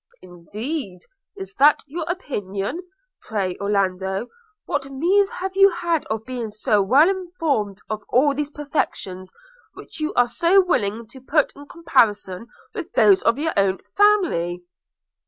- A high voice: Yes, very high, 265 Hz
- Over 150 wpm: No, average, 145 wpm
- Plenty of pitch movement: Yes, wide, 8.8 semitones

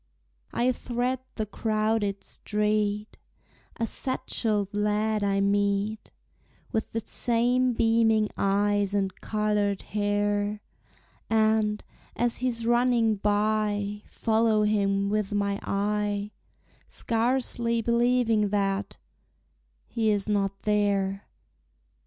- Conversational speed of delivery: No, slow, 95 wpm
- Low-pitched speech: No, high, 210 Hz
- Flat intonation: Yes, narrow, 1.7 semitones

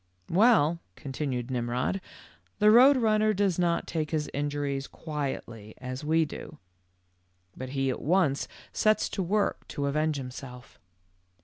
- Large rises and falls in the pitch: Yes, wide, 6.1 semitones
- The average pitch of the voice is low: No, medium, 150 Hz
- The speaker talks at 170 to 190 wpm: No, average, 140 wpm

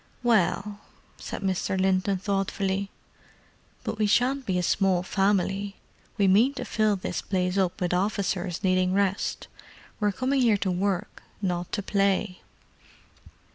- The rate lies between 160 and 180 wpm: No, slow, 135 wpm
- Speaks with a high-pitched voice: Yes, high, 195 Hz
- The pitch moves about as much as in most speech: No, narrow, 1.8 semitones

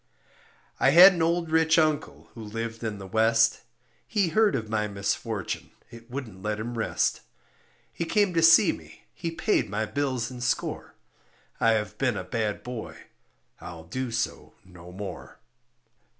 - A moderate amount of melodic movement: No, wide, 6.9 semitones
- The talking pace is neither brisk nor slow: Yes, average, 160 wpm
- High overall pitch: No, low, 115 Hz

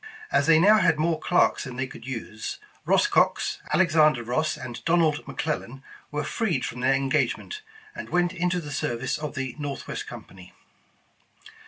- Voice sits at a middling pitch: Yes, medium, 150 Hz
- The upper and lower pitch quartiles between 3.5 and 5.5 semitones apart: Yes, average, 4.6 semitones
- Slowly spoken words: No, average, 160 wpm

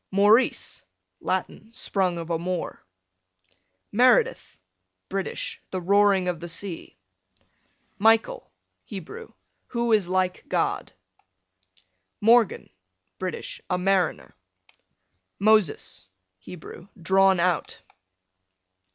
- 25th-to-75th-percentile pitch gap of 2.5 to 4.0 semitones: Yes, average, 3.4 semitones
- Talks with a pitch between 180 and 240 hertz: Yes, high, 190 Hz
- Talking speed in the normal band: No, slow, 85 wpm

